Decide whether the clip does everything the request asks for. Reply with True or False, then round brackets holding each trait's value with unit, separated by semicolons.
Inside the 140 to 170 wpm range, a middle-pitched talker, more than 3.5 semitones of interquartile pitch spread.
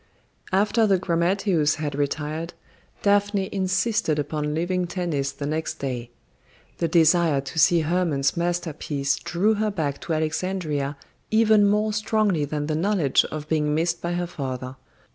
True (145 wpm; 165 Hz; 4.3 semitones)